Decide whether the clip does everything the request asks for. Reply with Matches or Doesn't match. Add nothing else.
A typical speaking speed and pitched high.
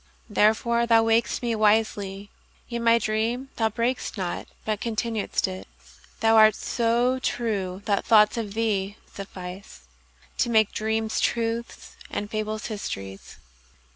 Doesn't match